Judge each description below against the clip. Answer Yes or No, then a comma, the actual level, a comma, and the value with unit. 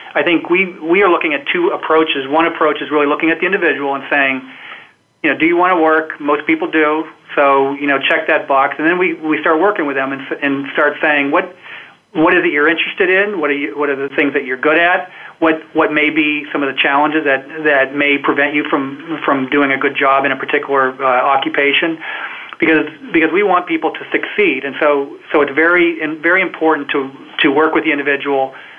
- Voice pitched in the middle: Yes, medium, 150 Hz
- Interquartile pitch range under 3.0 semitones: Yes, narrow, 2.6 semitones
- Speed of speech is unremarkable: No, fast, 225 wpm